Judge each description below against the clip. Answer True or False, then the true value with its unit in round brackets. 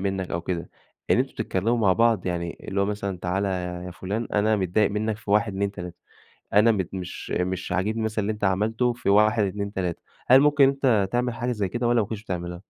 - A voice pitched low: True (100 Hz)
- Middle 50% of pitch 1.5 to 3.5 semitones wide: True (3.1 semitones)